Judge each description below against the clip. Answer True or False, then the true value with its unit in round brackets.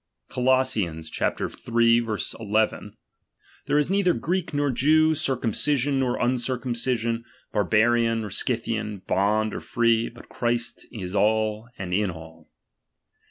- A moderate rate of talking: False (115 wpm)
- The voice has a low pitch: True (115 Hz)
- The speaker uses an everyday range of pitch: True (3.3 semitones)